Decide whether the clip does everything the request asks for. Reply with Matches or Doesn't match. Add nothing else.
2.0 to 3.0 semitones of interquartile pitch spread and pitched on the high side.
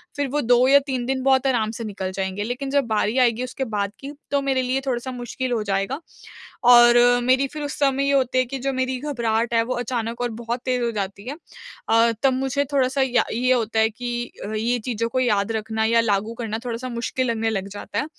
Matches